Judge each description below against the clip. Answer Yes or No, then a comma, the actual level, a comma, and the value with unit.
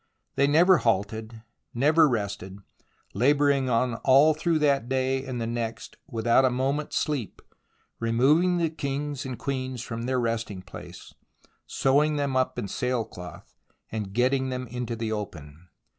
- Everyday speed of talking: Yes, average, 145 wpm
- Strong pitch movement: No, average, 3.6 semitones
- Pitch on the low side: Yes, low, 130 Hz